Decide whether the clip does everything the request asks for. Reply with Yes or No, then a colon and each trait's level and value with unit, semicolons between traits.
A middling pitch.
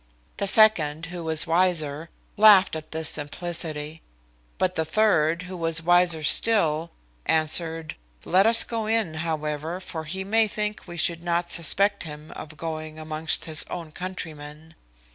Yes: medium, 165 Hz